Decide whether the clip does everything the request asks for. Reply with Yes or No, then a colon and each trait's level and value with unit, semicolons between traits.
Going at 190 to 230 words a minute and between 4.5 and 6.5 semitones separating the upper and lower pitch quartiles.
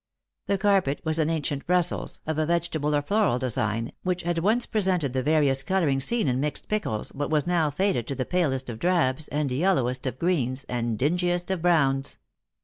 Yes: average, 195 wpm; average, 5.0 semitones